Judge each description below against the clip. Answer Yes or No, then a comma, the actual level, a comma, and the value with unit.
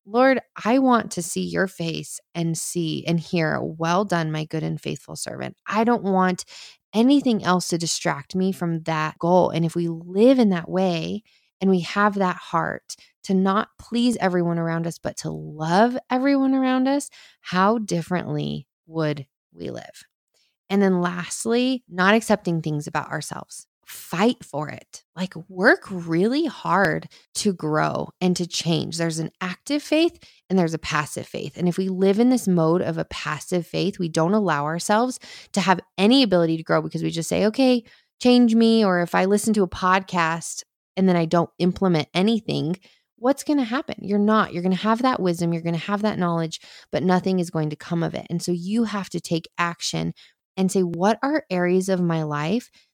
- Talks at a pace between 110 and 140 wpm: No, average, 190 wpm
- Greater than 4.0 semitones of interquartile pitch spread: Yes, average, 4.4 semitones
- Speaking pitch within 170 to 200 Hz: Yes, medium, 185 Hz